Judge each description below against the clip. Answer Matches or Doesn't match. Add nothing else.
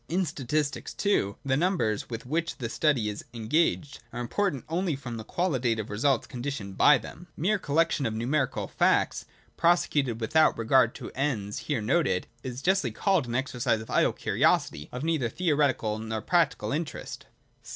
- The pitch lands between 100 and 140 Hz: Matches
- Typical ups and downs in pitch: Doesn't match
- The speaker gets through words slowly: Doesn't match